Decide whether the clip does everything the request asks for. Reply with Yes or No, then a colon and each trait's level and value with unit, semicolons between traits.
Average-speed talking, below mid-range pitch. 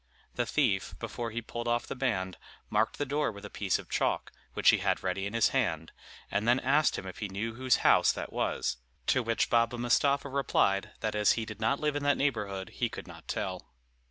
No: fast, 220 wpm; low, 115 Hz